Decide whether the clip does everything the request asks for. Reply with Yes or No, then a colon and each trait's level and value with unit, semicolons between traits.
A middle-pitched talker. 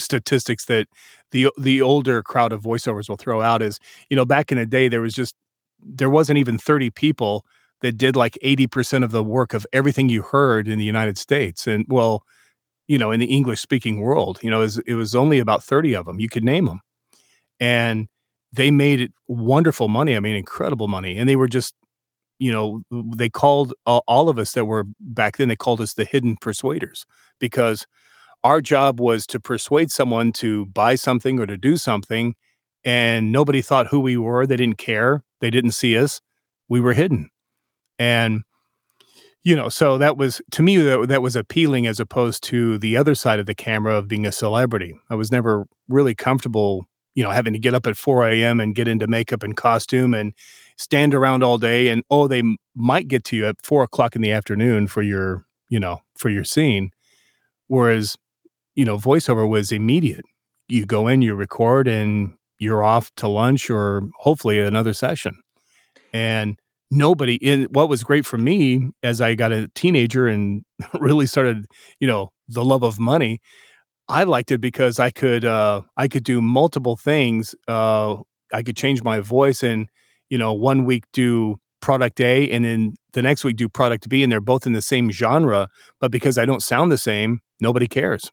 No: low, 120 Hz